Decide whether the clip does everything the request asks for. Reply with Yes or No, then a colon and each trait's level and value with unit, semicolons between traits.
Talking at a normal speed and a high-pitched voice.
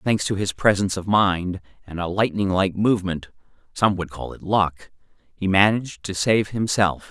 No: average, 175 wpm; very low, 95 Hz